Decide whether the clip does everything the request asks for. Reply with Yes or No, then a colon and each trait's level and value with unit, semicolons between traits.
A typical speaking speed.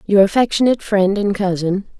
Yes: average, 150 wpm